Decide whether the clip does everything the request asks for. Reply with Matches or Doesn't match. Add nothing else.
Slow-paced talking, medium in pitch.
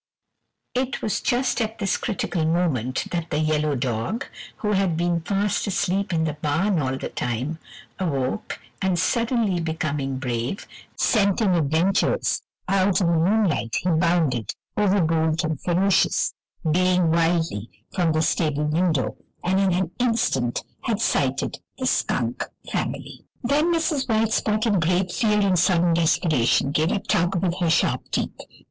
Doesn't match